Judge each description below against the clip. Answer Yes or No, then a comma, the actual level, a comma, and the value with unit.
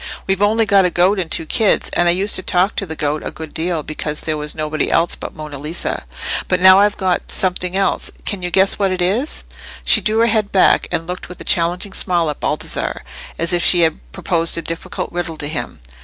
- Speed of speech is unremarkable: No, fast, 230 wpm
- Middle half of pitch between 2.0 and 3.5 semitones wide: Yes, average, 3.0 semitones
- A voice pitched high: No, medium, 180 Hz